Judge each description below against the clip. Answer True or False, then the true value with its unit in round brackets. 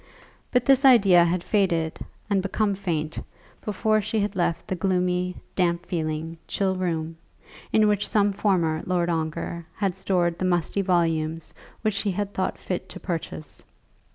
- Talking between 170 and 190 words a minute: False (155 wpm)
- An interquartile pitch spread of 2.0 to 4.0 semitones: True (3.1 semitones)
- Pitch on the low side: False (180 Hz)